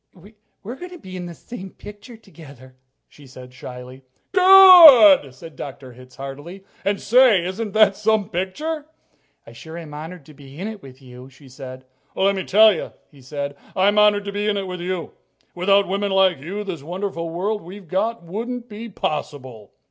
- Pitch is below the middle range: No, medium, 185 Hz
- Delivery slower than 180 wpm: No, average, 185 wpm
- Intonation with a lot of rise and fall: Yes, wide, 6.4 semitones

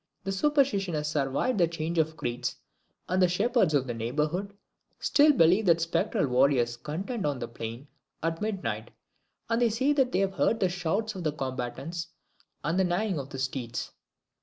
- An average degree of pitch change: No, wide, 6.5 semitones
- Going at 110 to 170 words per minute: No, average, 180 wpm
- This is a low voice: No, medium, 165 Hz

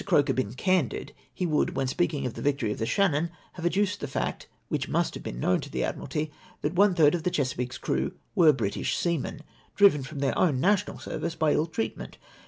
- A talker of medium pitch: Yes, medium, 150 Hz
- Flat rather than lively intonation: No, average, 5.0 semitones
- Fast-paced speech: Yes, fast, 215 wpm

